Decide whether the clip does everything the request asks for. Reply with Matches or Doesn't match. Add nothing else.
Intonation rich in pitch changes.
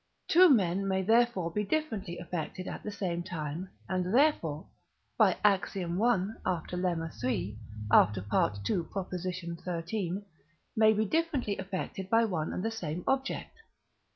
Doesn't match